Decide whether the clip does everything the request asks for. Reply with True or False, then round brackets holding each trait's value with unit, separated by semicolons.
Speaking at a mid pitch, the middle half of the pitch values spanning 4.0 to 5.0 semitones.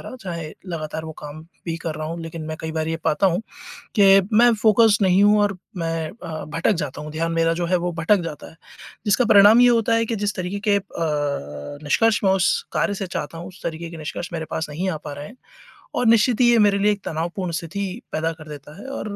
True (175 Hz; 4.3 semitones)